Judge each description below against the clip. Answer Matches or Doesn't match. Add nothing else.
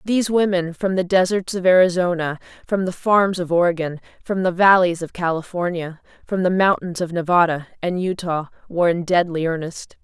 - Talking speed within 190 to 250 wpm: Doesn't match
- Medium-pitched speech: Matches